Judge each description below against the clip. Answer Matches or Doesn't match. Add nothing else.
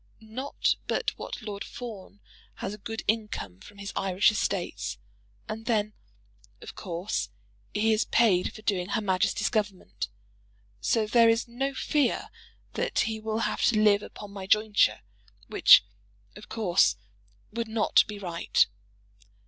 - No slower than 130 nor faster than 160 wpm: Matches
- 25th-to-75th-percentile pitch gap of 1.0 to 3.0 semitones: Matches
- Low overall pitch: Doesn't match